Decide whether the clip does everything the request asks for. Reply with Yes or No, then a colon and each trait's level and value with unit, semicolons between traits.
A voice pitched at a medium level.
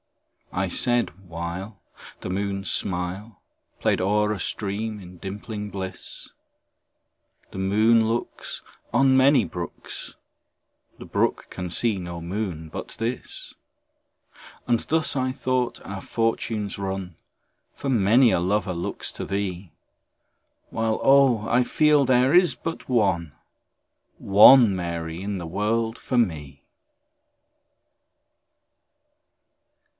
No: low, 105 Hz